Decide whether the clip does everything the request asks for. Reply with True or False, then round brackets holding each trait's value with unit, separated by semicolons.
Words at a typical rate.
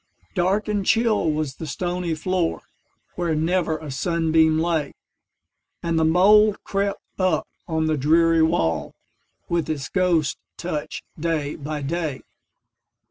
False (115 wpm)